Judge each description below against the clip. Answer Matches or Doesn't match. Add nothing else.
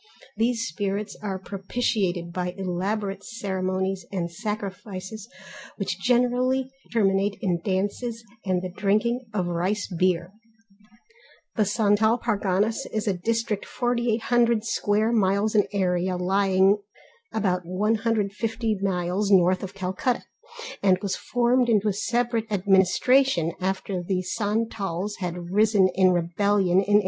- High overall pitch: Matches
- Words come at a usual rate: Doesn't match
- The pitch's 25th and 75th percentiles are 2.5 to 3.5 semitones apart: Matches